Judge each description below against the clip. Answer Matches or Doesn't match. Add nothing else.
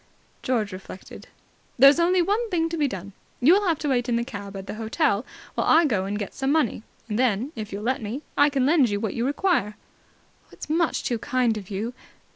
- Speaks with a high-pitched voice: Matches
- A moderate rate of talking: Doesn't match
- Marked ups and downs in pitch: Matches